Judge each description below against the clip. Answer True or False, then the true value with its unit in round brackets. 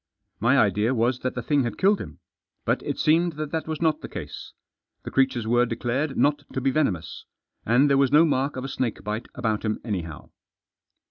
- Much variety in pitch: False (4.2 semitones)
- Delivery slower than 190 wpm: False (205 wpm)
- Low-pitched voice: True (130 Hz)